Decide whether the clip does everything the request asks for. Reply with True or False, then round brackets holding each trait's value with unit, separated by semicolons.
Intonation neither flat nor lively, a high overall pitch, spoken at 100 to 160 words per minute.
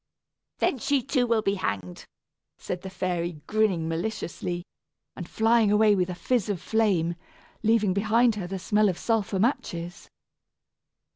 True (3.9 semitones; 200 Hz; 145 wpm)